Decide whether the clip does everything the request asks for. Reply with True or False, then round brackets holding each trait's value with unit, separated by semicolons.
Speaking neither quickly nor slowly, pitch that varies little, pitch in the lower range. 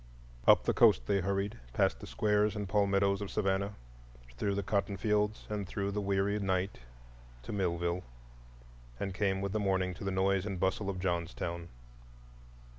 True (165 wpm; 1.4 semitones; 100 Hz)